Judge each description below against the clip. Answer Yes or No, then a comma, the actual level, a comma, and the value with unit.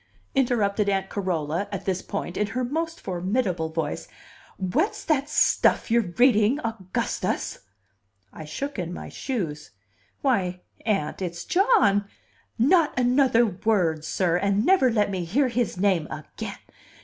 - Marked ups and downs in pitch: Yes, wide, 5.9 semitones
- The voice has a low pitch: No, high, 205 Hz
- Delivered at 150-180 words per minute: No, slow, 135 wpm